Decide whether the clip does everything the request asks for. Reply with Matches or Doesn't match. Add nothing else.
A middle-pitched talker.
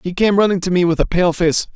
Matches